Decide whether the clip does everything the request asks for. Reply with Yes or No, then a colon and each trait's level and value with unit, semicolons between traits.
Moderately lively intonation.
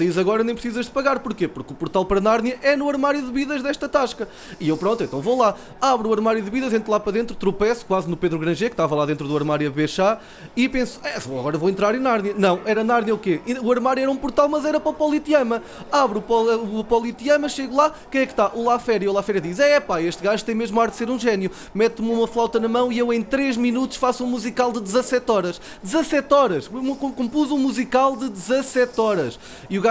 Yes: average, 4.2 semitones